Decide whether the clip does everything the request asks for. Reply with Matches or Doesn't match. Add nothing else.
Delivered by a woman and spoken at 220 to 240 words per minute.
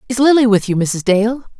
Matches